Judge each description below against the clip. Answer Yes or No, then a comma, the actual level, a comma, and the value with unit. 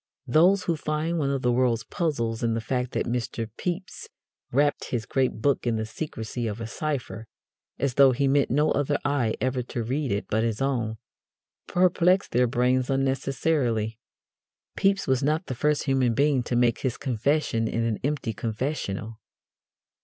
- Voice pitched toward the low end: Yes, low, 130 Hz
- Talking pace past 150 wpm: Yes, average, 170 wpm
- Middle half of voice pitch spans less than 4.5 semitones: Yes, average, 4.0 semitones